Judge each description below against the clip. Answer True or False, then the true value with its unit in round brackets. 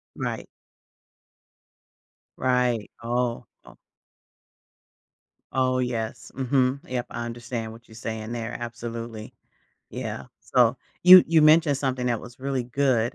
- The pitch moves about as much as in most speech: False (1.9 semitones)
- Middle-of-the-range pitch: False (120 Hz)